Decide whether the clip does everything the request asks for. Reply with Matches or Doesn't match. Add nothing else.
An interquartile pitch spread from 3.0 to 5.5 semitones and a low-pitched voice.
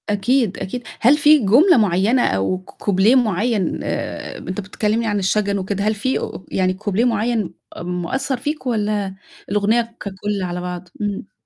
Doesn't match